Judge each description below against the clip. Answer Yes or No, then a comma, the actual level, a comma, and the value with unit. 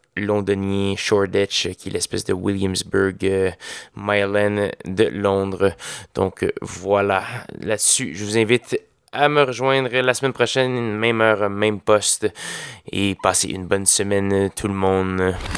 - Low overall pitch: Yes, low, 100 Hz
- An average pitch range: No, narrow, 2.3 semitones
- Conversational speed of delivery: No, slow, 135 wpm